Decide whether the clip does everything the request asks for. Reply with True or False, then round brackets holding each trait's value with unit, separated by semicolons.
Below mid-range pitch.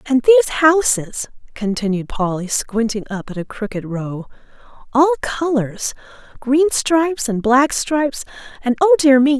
False (255 Hz)